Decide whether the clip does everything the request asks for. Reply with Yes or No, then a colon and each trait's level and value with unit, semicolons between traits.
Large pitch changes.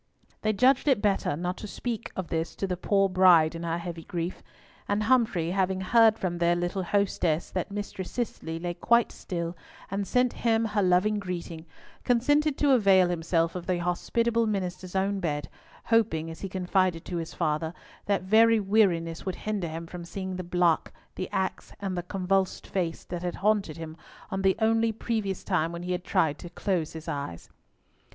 No: average, 3.3 semitones